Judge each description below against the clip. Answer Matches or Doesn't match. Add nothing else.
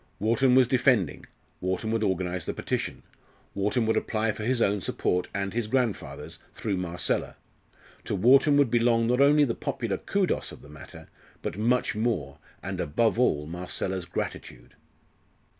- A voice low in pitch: Matches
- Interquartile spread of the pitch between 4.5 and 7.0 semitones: Matches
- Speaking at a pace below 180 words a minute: Matches